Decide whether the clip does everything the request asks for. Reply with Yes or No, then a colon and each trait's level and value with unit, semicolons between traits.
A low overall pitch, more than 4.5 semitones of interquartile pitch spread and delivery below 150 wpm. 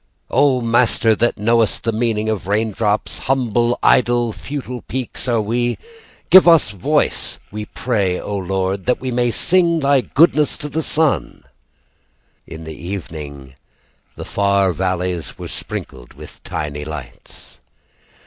Yes: low, 110 Hz; average, 5.0 semitones; average, 140 wpm